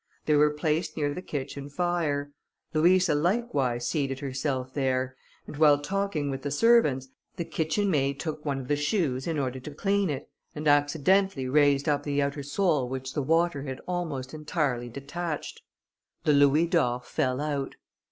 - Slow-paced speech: No, average, 165 wpm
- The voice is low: No, medium, 145 Hz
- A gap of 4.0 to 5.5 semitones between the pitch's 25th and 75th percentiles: No, average, 3.3 semitones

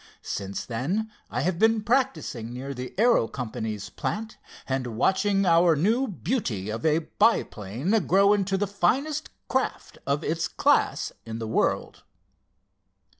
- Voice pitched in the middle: Yes, medium, 170 Hz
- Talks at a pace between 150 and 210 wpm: No, slow, 135 wpm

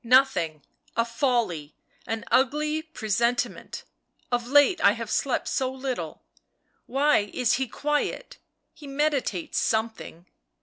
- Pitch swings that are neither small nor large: Yes, average, 4.2 semitones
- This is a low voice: No, very high, 250 Hz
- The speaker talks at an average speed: No, slow, 125 wpm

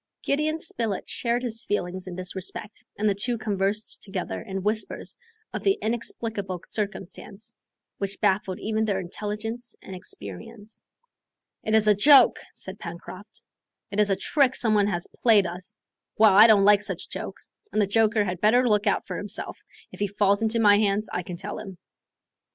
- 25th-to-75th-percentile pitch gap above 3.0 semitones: No, narrow, 2.4 semitones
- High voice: Yes, high, 210 Hz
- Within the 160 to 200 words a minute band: Yes, average, 175 wpm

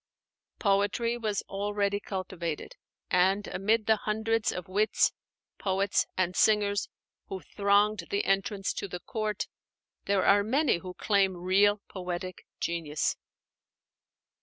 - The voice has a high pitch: Yes, high, 200 Hz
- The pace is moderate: No, slow, 115 wpm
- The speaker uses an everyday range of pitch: No, narrow, 2.1 semitones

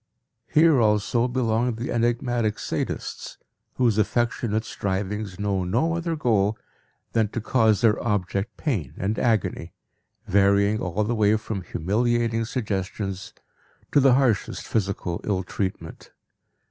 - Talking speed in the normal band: No, slow, 120 wpm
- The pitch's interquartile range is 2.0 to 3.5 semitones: Yes, average, 3.2 semitones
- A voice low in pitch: Yes, low, 110 Hz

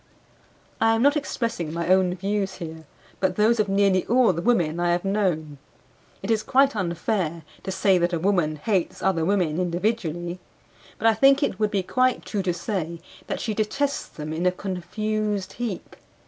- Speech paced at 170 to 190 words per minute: Yes, average, 180 wpm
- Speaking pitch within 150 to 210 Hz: Yes, high, 190 Hz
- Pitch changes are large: No, average, 3.9 semitones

